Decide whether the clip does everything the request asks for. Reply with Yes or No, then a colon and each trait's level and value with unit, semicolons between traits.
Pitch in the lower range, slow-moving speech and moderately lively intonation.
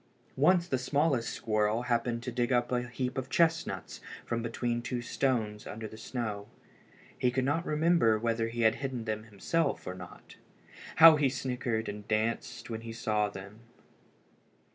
No: low, 120 Hz; average, 165 wpm; average, 3.1 semitones